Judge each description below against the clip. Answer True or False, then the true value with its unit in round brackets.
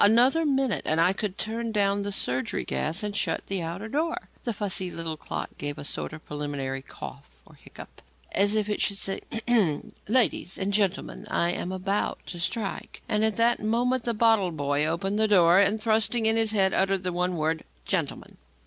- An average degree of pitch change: True (4.4 semitones)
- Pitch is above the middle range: True (200 Hz)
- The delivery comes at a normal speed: True (195 wpm)